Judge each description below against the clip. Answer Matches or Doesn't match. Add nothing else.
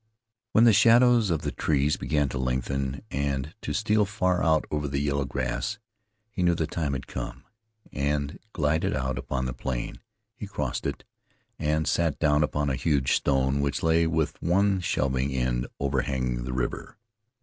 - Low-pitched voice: Matches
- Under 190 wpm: Matches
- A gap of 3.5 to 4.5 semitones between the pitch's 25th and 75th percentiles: Matches